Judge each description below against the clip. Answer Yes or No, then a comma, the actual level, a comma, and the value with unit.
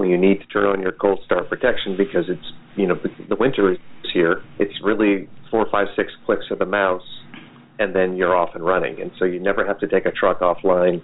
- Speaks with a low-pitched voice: Yes, very low, 95 Hz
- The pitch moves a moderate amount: No, narrow, 1.4 semitones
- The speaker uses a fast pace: Yes, fast, 235 wpm